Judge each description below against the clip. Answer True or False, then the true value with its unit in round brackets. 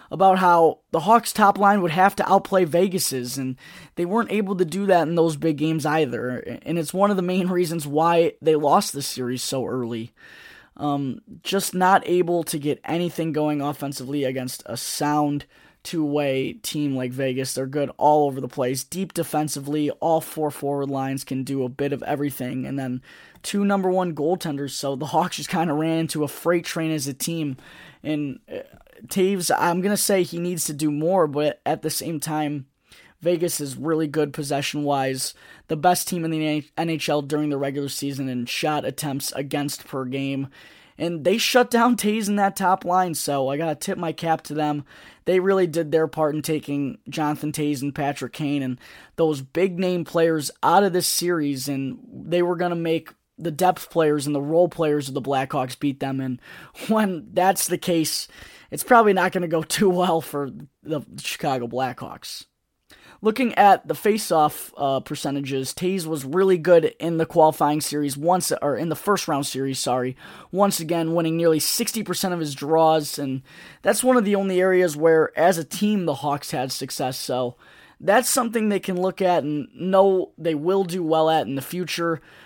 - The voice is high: False (160 Hz)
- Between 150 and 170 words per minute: False (190 wpm)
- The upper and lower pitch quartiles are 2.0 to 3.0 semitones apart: False (4.0 semitones)